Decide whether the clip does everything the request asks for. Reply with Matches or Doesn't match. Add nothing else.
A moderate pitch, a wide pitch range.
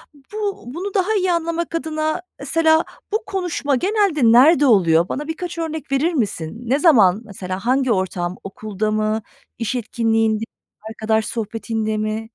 Doesn't match